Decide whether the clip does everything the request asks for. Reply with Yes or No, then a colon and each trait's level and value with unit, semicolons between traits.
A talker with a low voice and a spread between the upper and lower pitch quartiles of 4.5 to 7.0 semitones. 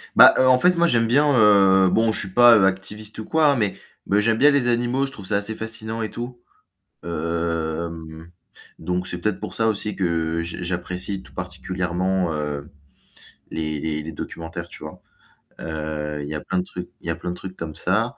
Yes: very low, 95 Hz; average, 5.2 semitones